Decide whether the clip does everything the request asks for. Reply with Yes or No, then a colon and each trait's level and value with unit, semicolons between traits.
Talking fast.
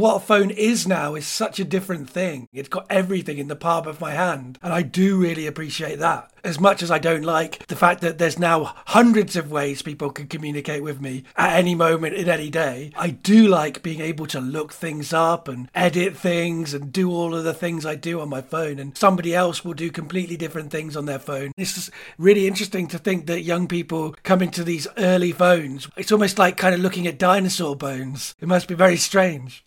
Yes: fast, 225 wpm